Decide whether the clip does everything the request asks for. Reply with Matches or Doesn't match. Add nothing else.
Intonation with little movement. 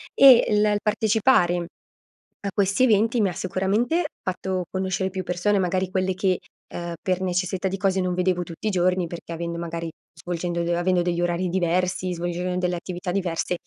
Matches